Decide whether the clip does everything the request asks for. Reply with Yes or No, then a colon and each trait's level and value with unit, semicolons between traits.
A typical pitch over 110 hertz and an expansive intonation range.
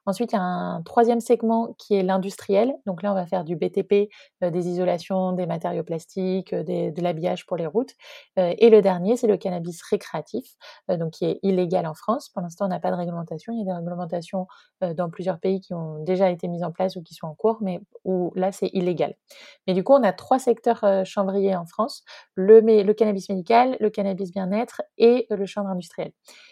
No: high, 190 Hz; average, 3.3 semitones